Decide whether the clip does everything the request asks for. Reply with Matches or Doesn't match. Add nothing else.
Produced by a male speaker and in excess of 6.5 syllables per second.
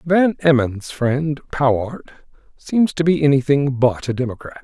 Doesn't match